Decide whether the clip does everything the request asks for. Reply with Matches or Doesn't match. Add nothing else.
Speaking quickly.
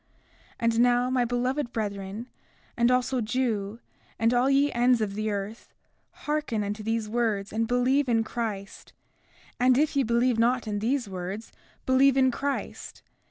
Doesn't match